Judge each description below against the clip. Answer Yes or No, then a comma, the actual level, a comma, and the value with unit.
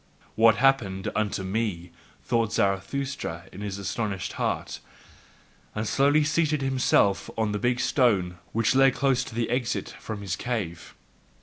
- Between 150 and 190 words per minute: No, average, 140 wpm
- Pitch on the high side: No, low, 110 Hz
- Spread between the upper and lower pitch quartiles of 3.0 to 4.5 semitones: No, average, 5.0 semitones